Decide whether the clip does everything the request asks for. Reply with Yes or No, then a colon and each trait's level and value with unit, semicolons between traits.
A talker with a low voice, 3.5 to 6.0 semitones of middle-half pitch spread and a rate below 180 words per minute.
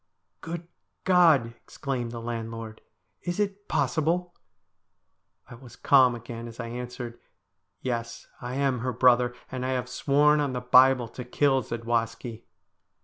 No: low, 125 Hz; average, 3.0 semitones; average, 155 wpm